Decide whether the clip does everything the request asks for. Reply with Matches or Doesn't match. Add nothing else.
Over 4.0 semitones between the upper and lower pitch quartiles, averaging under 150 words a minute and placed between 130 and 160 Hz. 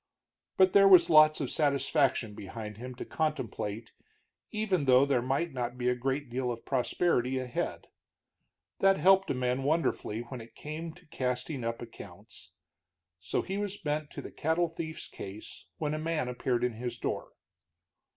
Doesn't match